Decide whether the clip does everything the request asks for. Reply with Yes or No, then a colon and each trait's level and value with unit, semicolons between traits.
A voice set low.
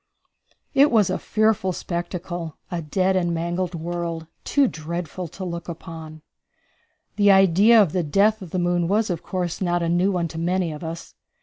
No: medium, 175 Hz